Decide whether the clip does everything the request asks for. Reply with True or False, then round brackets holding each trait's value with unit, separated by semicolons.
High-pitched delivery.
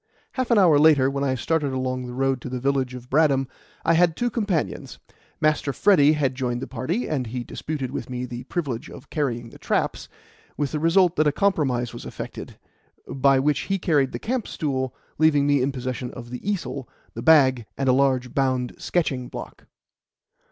False (135 Hz)